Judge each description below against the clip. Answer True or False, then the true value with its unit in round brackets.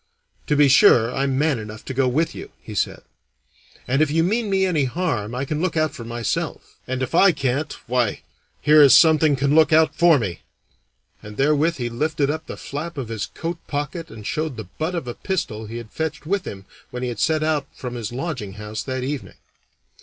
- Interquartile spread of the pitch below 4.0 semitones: False (4.8 semitones)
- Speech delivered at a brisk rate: True (215 wpm)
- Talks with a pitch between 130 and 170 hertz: True (140 Hz)